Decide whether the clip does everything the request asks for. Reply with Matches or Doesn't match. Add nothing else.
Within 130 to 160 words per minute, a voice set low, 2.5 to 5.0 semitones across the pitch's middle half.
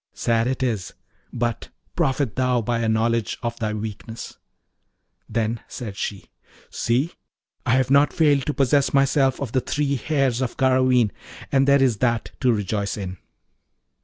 Matches